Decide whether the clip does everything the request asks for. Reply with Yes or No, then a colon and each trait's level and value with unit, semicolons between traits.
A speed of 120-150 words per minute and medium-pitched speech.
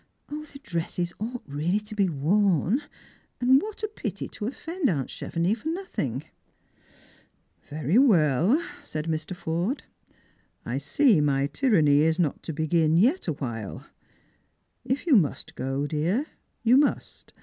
Yes: average, 140 wpm; medium, 175 Hz